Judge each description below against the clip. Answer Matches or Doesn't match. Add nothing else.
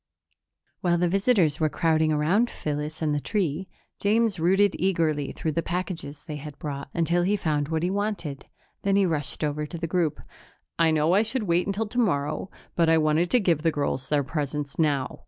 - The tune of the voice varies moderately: Matches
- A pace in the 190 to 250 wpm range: Matches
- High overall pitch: Doesn't match